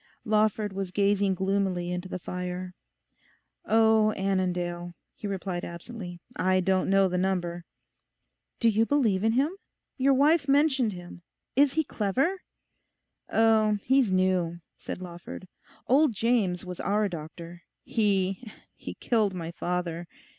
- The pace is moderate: No, slow, 125 wpm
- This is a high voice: Yes, high, 195 Hz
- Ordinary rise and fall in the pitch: Yes, average, 3.8 semitones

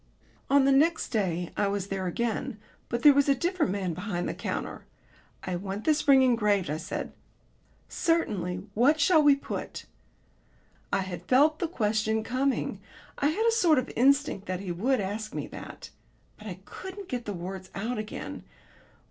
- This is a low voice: No, high, 225 Hz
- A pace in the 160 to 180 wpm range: Yes, average, 175 wpm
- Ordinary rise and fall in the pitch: No, wide, 6.6 semitones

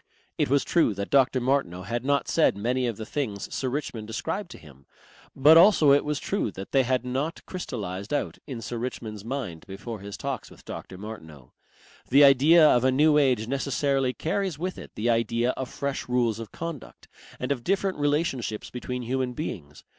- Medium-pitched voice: No, low, 125 Hz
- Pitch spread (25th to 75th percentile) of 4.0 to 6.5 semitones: Yes, average, 4.5 semitones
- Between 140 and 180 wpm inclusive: No, average, 190 wpm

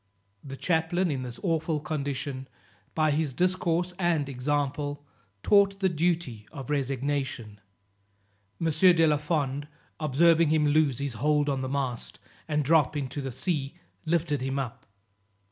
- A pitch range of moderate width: Yes, average, 3.3 semitones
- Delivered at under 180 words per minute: Yes, average, 140 wpm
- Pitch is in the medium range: Yes, medium, 150 Hz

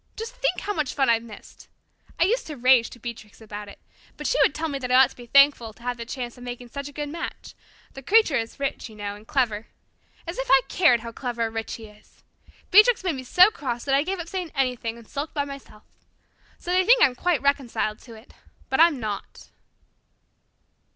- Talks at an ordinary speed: No, fast, 230 wpm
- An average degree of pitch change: No, wide, 5.8 semitones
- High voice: Yes, very high, 265 Hz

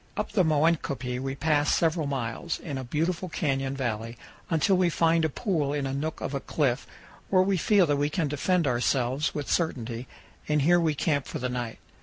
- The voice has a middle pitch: Yes, medium, 145 Hz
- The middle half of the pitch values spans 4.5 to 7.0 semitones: No, average, 3.7 semitones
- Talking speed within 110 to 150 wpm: No, average, 200 wpm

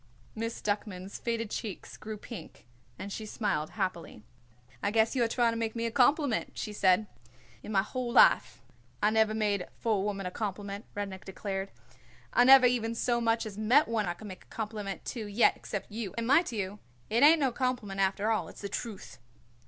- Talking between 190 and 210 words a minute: Yes, average, 200 wpm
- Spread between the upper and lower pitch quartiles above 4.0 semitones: No, narrow, 2.6 semitones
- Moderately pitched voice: No, high, 215 Hz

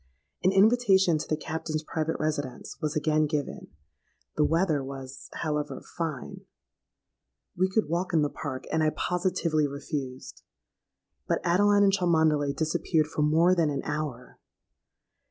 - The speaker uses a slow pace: Yes, slow, 130 wpm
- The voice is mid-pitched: Yes, medium, 155 Hz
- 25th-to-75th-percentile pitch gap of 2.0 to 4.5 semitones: Yes, average, 2.9 semitones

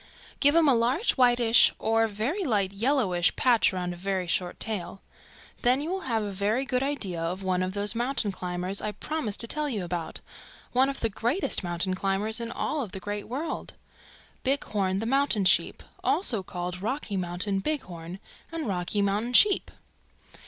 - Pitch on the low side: No, high, 215 Hz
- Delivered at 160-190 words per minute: Yes, average, 175 wpm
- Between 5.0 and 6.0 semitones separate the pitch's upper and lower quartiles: Yes, wide, 5.5 semitones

